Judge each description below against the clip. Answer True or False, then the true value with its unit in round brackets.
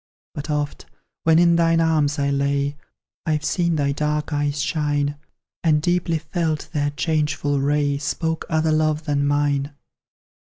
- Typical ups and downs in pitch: False (1.9 semitones)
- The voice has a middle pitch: True (150 Hz)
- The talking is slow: False (145 wpm)